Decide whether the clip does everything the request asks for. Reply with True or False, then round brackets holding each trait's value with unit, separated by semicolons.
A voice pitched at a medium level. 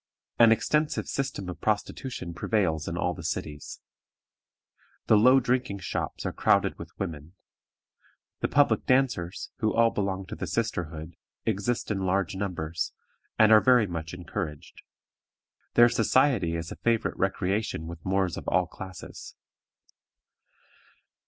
False (95 Hz)